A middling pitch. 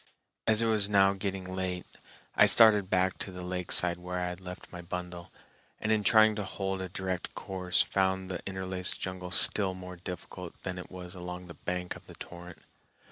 No: very low, 95 Hz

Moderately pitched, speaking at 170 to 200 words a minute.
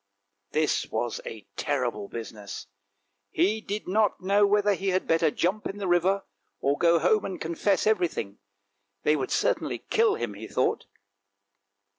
No: medium, 175 Hz; average, 155 wpm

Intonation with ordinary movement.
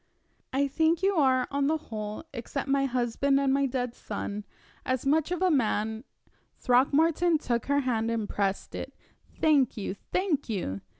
Yes: average, 4.2 semitones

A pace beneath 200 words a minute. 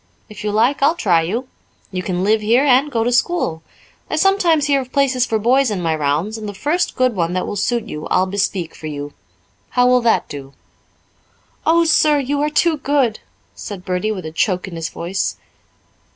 No: fast, 205 wpm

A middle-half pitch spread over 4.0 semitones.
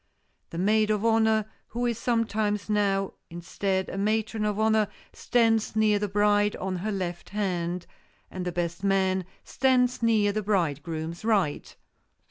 No: narrow, 2.6 semitones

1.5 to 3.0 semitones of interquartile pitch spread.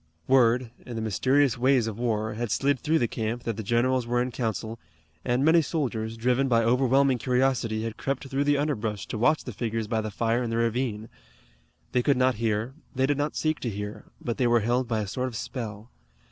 Yes: average, 2.7 semitones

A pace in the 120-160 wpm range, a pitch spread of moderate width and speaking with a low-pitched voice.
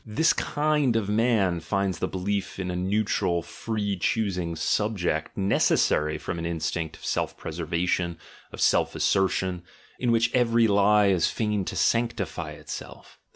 Yes: average, 145 wpm; average, 4.1 semitones; low, 100 Hz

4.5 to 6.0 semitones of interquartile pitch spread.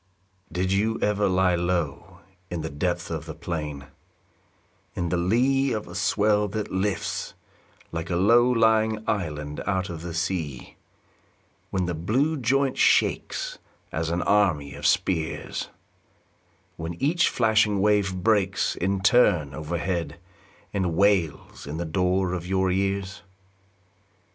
No: average, 3.7 semitones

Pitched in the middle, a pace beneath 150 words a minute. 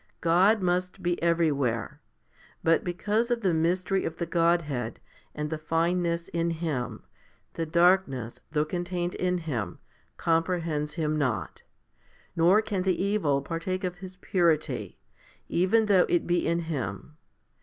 Yes: medium, 170 Hz; slow, 135 wpm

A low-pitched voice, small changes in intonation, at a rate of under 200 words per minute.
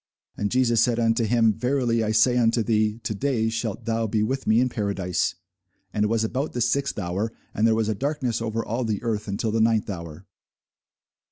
No: low, 115 Hz; narrow, 2.0 semitones; fast, 205 wpm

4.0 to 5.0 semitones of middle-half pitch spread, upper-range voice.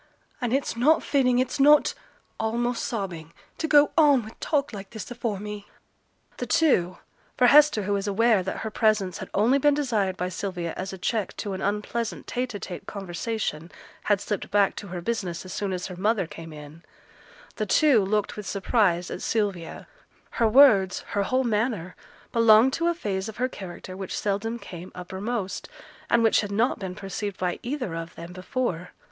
Yes: average, 4.3 semitones; high, 210 Hz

